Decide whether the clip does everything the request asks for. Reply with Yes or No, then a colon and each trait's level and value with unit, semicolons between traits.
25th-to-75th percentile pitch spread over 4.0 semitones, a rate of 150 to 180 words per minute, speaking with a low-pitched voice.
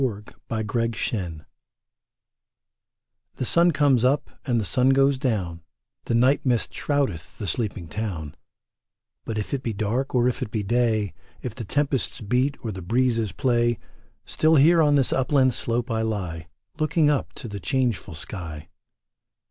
Yes: average, 4.5 semitones; average, 155 wpm; low, 120 Hz